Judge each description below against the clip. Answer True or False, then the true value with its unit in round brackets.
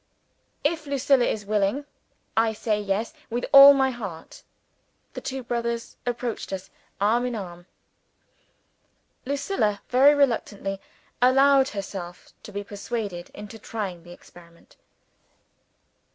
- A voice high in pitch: True (225 Hz)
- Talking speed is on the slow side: True (115 wpm)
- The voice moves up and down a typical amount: True (4.7 semitones)